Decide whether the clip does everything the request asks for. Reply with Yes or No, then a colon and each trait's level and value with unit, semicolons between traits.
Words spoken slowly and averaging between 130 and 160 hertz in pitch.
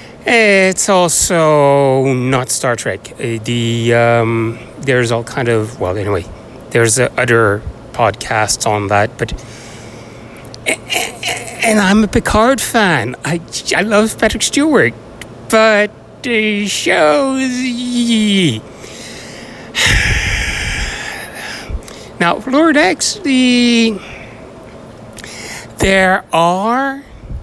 Yes: slow, 85 wpm; medium, 140 Hz